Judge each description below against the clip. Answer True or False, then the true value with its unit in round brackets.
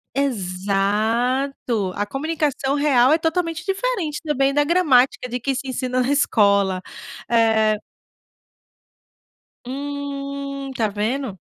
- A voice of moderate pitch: False (270 Hz)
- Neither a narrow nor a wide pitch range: True (4.6 semitones)